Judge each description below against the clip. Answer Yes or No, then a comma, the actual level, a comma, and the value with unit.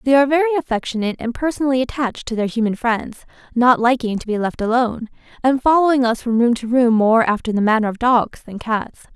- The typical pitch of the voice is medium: No, high, 240 Hz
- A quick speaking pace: Yes, fast, 210 wpm